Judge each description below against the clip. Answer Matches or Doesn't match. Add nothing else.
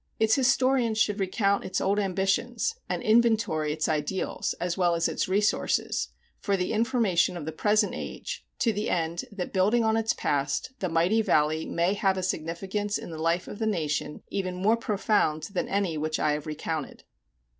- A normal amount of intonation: Matches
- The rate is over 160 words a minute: Matches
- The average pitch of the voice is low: Doesn't match